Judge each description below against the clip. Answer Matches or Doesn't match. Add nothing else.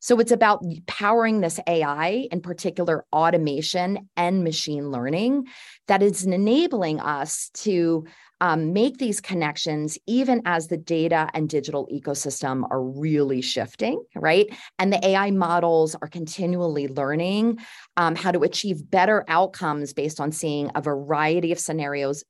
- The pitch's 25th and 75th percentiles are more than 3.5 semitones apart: Matches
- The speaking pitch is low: Doesn't match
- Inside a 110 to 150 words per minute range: Matches